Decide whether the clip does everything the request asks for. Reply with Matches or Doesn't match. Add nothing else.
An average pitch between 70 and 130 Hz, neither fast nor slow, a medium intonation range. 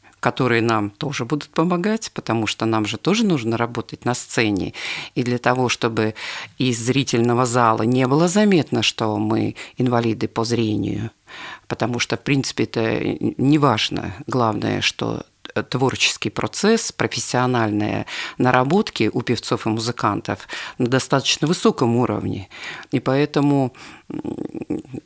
Matches